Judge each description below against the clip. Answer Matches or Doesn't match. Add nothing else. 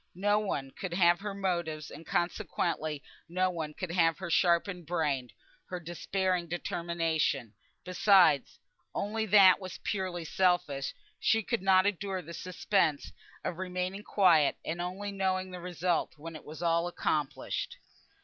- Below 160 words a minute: Matches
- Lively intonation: Doesn't match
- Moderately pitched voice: Matches